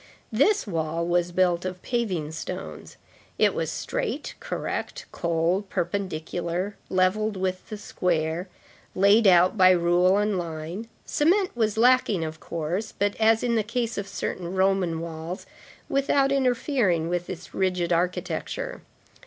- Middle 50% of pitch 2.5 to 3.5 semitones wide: No, average, 4.3 semitones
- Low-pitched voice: No, medium, 185 Hz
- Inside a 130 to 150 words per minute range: Yes, slow, 135 wpm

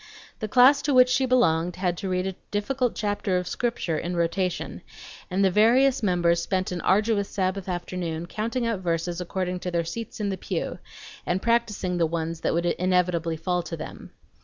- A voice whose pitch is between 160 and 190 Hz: Yes, medium, 185 Hz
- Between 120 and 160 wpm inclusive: No, average, 185 wpm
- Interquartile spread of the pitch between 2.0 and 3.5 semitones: No, average, 3.9 semitones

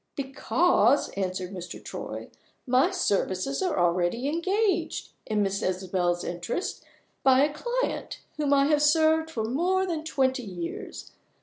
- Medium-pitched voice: No, very high, 270 Hz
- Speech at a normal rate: No, slow, 130 wpm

